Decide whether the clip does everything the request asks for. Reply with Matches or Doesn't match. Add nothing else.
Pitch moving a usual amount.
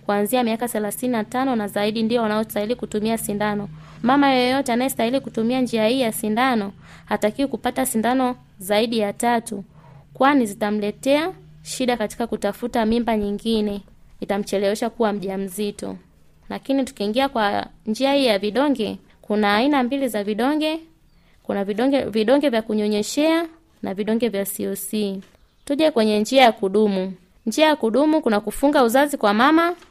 Matches